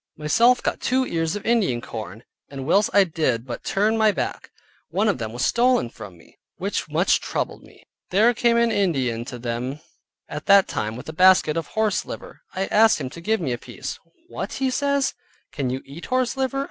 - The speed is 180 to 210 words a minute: Yes, fast, 205 wpm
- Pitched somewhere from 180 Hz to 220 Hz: Yes, medium, 185 Hz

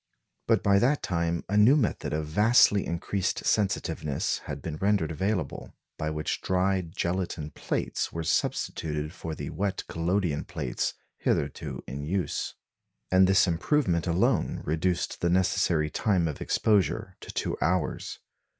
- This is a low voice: Yes, very low, 90 Hz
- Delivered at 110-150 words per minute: Yes, average, 140 wpm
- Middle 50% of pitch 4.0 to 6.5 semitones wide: No, average, 3.6 semitones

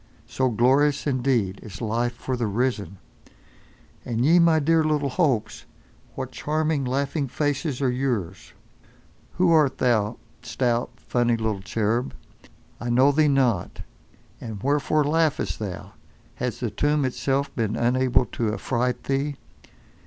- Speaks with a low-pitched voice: Yes, low, 130 Hz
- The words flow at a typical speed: No, slow, 130 wpm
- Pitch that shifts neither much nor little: Yes, average, 3.6 semitones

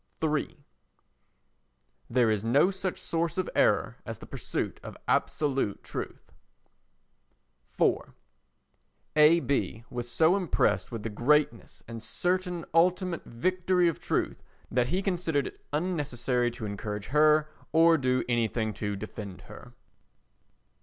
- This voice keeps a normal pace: No, slow, 125 wpm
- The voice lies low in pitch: No, medium, 145 Hz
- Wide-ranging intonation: Yes, wide, 6.4 semitones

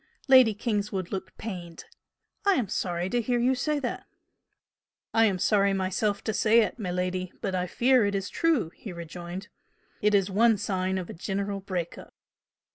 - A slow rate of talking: No, average, 175 wpm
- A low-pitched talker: No, high, 200 Hz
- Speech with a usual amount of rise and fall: Yes, average, 3.5 semitones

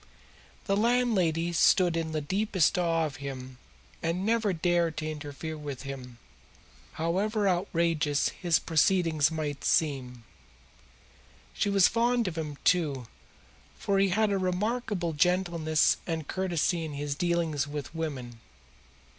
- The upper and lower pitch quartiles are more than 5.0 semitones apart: No, average, 4.1 semitones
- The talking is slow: Yes, slow, 130 wpm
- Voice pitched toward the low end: No, medium, 165 Hz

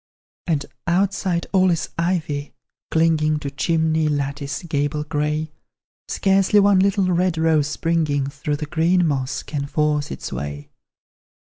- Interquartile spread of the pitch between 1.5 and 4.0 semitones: Yes, average, 3.0 semitones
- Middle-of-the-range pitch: Yes, medium, 155 Hz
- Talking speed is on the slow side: Yes, slow, 130 wpm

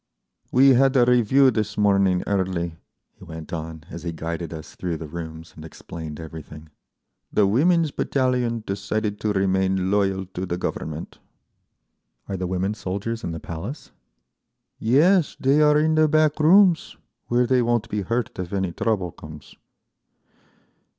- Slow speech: No, average, 155 wpm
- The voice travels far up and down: Yes, wide, 6.6 semitones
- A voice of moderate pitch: No, low, 100 Hz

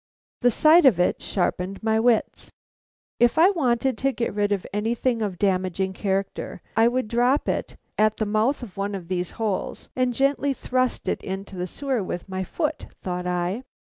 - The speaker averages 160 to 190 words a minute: Yes, average, 185 wpm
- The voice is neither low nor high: No, high, 215 Hz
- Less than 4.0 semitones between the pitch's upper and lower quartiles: No, average, 4.9 semitones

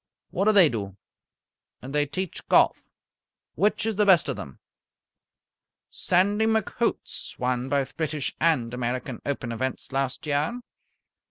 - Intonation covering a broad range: Yes, wide, 7.0 semitones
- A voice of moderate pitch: Yes, medium, 145 Hz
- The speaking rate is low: Yes, slow, 125 wpm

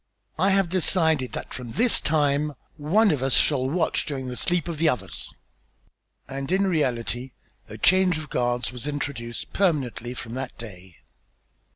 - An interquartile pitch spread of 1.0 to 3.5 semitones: No, average, 5.1 semitones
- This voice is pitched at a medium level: Yes, medium, 145 Hz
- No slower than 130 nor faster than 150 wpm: No, average, 160 wpm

